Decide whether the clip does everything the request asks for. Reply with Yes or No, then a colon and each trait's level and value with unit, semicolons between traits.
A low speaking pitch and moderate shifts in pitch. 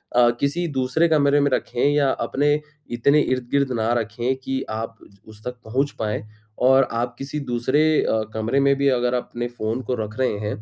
Yes: low, 125 Hz; average, 3.4 semitones